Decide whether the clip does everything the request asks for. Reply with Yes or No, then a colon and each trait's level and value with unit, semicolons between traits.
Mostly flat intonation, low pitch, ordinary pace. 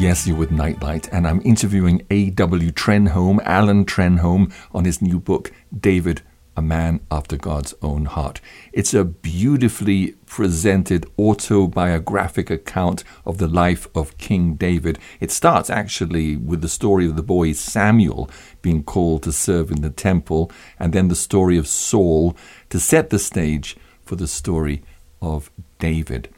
No: average, 3.4 semitones; very low, 85 Hz; average, 150 wpm